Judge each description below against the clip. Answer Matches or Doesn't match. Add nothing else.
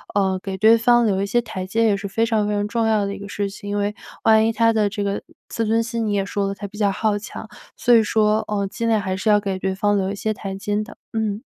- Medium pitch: Doesn't match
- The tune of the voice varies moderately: Doesn't match